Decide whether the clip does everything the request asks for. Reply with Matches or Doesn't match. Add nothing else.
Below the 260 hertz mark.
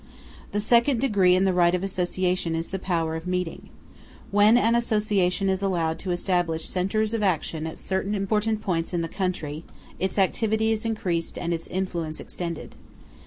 Matches